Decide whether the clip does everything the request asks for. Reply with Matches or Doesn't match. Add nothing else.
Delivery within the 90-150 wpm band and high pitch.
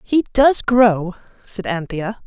Matches